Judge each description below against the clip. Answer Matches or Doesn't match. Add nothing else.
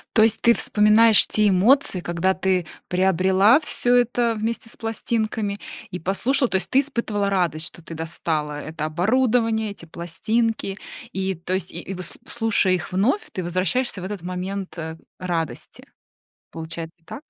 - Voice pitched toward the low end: Doesn't match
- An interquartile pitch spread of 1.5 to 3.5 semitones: Doesn't match